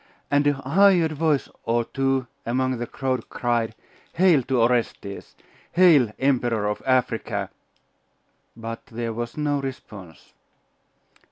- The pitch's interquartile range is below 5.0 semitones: Yes, average, 3.7 semitones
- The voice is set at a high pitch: No, low, 130 Hz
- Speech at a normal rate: No, slow, 115 wpm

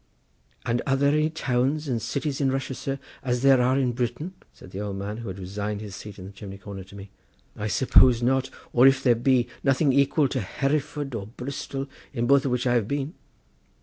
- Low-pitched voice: Yes, low, 125 Hz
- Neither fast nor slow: No, fast, 215 wpm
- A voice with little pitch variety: No, average, 4.4 semitones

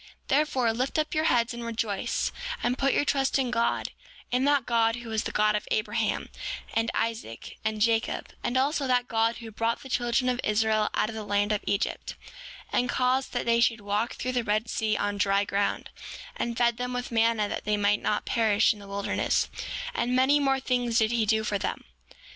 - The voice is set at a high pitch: Yes, high, 230 Hz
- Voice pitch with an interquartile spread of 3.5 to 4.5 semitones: No, average, 2.8 semitones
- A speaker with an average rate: No, fast, 210 wpm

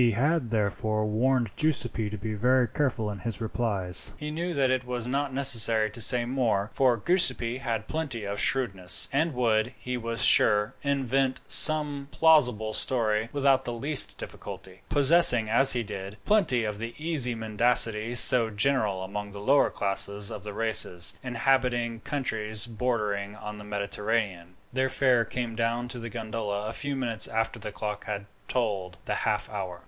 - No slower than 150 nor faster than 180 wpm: Yes, average, 165 wpm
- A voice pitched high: No, low, 115 Hz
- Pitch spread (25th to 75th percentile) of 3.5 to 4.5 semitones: Yes, average, 3.8 semitones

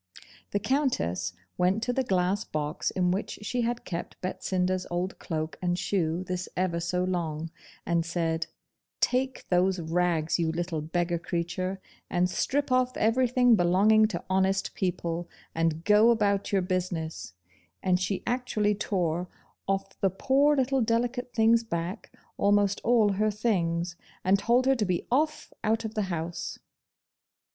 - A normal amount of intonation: Yes, average, 4.4 semitones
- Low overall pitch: No, high, 190 Hz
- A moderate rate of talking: Yes, average, 150 wpm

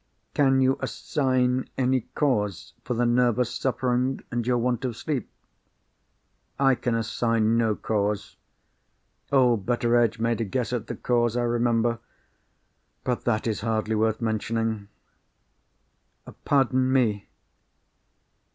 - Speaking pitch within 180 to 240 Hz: No, low, 120 Hz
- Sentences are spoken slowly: Yes, slow, 120 wpm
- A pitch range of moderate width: No, narrow, 2.1 semitones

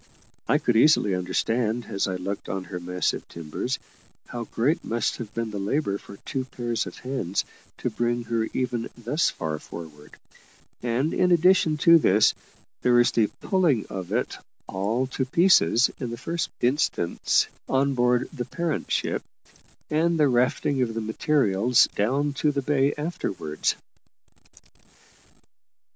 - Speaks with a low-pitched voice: Yes, low, 120 Hz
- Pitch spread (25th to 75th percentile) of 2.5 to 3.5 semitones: No, wide, 5.6 semitones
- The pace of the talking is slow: No, average, 150 wpm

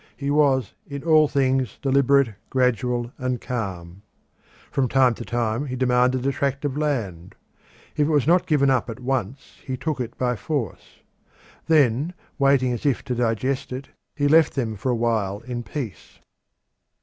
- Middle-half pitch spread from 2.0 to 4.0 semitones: Yes, average, 2.8 semitones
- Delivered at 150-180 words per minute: Yes, average, 165 wpm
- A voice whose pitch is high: No, low, 130 Hz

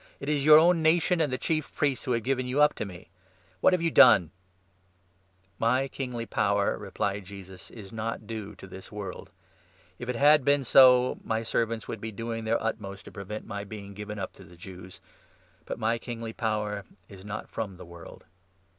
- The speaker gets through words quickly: Yes, fast, 210 wpm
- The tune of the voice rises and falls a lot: No, average, 4.4 semitones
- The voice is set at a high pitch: No, low, 110 Hz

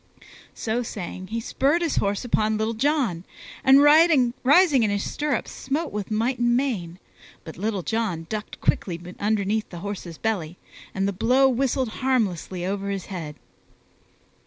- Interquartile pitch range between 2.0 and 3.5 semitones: No, average, 5.1 semitones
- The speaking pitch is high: Yes, high, 220 Hz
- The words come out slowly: No, average, 150 wpm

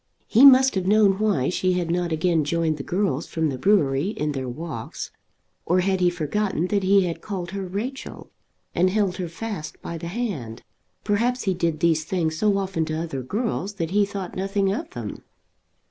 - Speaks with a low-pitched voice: No, medium, 185 Hz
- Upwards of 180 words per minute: Yes, average, 190 wpm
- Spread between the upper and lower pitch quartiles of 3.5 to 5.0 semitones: Yes, average, 4.0 semitones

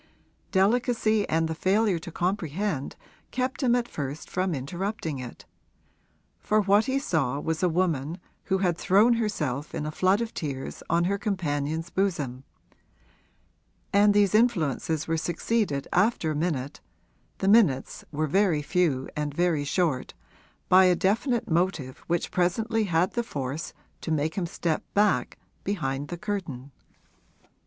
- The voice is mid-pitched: Yes, medium, 175 Hz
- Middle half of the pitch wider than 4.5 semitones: Yes, average, 5.3 semitones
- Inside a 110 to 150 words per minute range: Yes, average, 145 wpm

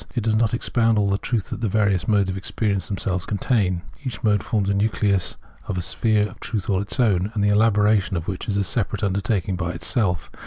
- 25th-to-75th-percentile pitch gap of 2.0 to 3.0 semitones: Yes, narrow, 2.4 semitones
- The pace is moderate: No, fast, 220 wpm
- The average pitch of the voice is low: Yes, low, 100 Hz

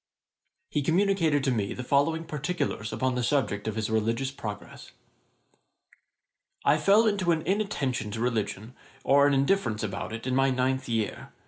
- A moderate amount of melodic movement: No, wide, 5.8 semitones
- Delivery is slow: No, average, 160 wpm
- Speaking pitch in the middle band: No, low, 130 Hz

